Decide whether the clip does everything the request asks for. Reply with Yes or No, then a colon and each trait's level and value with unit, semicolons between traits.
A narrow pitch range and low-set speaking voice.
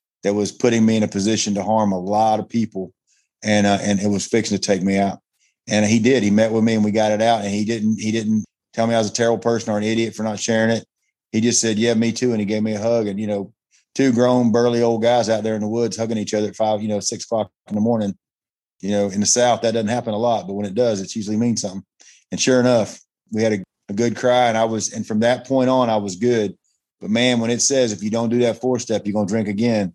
Yes: narrow, 2.0 semitones; low, 110 Hz